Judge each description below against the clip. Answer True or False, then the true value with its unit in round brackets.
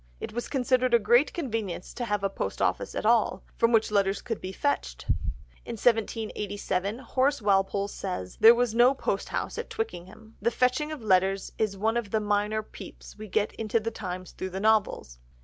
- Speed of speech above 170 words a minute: True (185 wpm)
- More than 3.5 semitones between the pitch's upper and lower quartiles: False (3.2 semitones)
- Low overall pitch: False (220 Hz)